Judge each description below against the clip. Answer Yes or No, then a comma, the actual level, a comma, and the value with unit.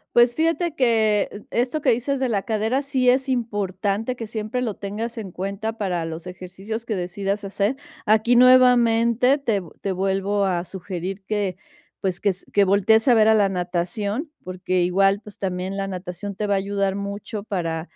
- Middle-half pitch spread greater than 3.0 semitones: Yes, average, 3.4 semitones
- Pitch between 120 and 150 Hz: No, high, 205 Hz